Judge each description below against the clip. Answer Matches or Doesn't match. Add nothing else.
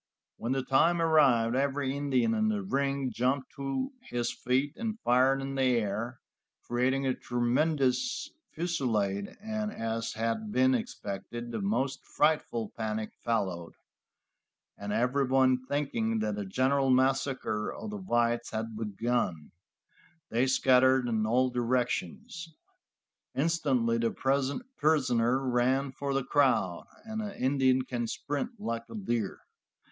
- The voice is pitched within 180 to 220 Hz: Doesn't match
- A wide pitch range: Doesn't match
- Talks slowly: Matches